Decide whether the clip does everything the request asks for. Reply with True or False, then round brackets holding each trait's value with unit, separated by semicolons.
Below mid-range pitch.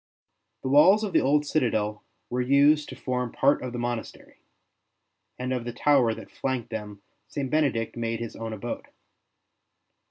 True (125 Hz)